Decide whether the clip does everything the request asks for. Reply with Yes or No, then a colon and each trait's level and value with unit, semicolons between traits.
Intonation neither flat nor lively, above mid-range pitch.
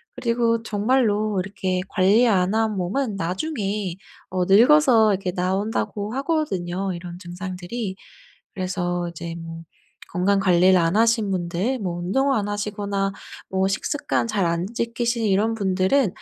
Yes: average, 3.7 semitones; high, 195 Hz